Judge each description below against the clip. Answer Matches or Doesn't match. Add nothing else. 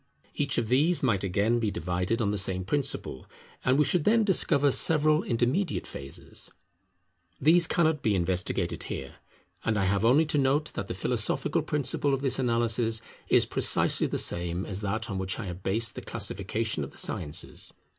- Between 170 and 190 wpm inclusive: Matches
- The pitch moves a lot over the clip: Matches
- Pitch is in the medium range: Doesn't match